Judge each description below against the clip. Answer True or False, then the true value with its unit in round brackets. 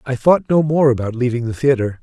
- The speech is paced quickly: True (235 wpm)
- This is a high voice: False (130 Hz)